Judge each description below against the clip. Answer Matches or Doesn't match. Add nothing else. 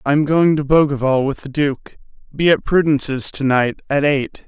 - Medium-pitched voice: Matches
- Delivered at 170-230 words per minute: Matches